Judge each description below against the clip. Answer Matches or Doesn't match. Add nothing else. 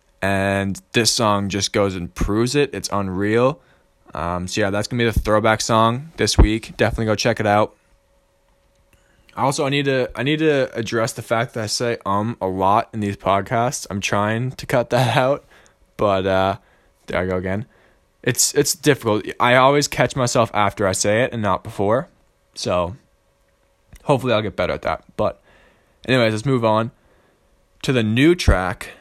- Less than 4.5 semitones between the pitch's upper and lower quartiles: Matches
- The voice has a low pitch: Matches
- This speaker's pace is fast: Doesn't match